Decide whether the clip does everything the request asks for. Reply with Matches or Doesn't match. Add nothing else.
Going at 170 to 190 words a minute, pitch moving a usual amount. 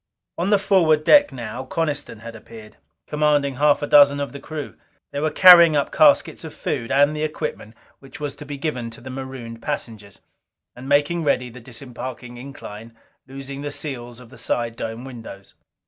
Matches